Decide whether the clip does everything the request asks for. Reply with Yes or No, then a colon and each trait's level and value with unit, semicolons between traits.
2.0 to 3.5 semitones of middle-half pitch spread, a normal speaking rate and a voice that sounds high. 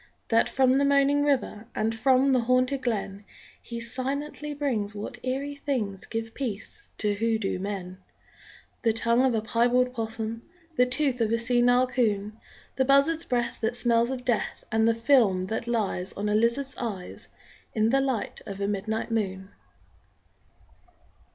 Yes: average, 3.1 semitones; average, 155 wpm; high, 235 Hz